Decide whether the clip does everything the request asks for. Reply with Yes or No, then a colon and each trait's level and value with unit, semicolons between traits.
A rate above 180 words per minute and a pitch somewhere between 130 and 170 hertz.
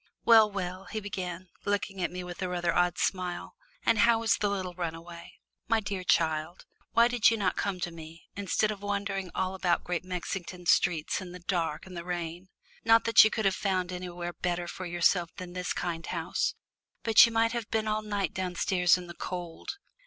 No: average, 200 wpm; medium, 185 Hz